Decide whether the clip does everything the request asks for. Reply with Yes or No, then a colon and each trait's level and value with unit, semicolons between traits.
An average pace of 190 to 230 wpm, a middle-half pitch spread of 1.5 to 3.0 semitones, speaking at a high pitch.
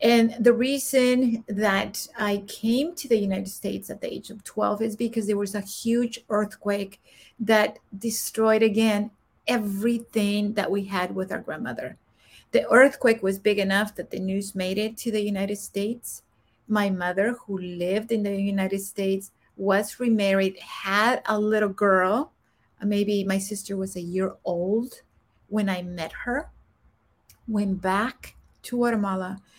No: average, 150 wpm; narrow, 2.6 semitones; high, 205 Hz